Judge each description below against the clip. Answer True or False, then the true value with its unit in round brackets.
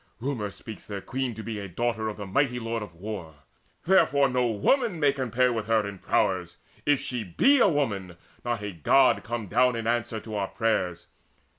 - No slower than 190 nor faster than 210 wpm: True (195 wpm)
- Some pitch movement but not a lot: True (3.8 semitones)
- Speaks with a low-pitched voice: True (115 Hz)